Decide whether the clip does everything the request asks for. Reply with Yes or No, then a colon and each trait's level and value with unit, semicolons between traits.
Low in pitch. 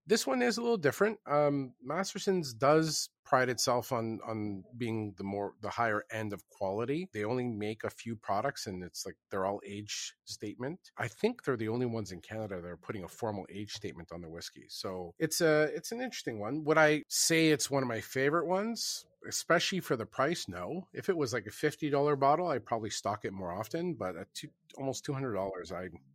Yes: low, 125 Hz